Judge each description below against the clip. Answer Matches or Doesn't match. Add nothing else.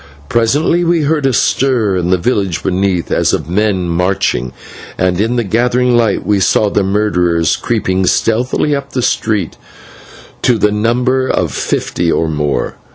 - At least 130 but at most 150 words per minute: Doesn't match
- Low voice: Matches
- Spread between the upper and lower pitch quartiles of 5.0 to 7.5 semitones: Matches